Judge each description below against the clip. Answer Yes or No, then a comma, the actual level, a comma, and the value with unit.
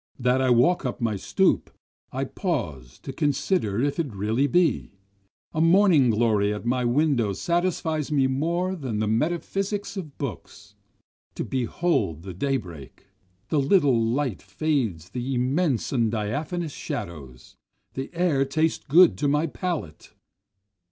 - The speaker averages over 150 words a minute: No, average, 140 wpm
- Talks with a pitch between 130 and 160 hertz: Yes, low, 135 Hz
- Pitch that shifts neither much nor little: No, wide, 6.3 semitones